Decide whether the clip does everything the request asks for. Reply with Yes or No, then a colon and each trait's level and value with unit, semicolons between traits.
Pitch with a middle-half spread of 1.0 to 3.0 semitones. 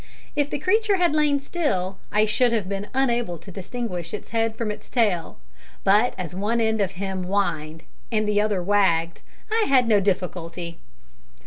No: average, 4.8 semitones